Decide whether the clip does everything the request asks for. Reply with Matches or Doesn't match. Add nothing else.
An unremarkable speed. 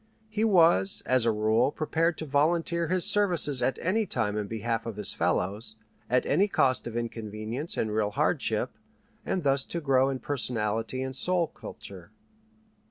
Matches